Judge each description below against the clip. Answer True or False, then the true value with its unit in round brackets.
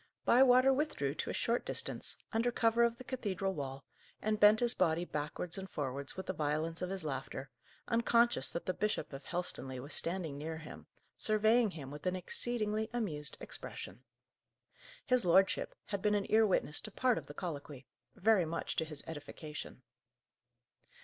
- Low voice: False (185 Hz)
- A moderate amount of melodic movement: False (6.7 semitones)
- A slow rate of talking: False (170 wpm)